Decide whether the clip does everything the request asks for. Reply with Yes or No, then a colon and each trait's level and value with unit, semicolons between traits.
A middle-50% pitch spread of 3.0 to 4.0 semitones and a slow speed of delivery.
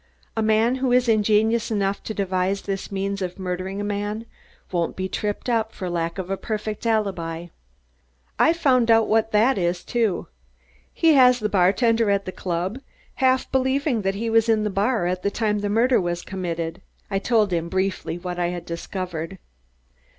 No: average, 3.6 semitones; average, 180 wpm